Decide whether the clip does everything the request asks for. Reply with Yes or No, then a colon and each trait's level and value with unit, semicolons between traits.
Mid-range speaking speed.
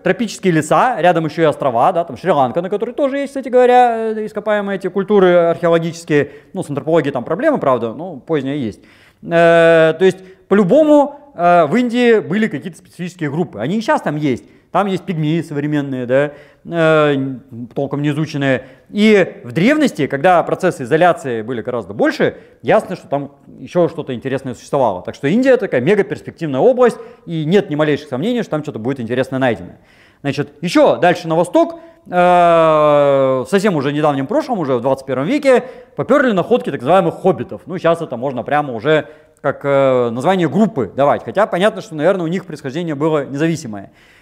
No: fast, 165 wpm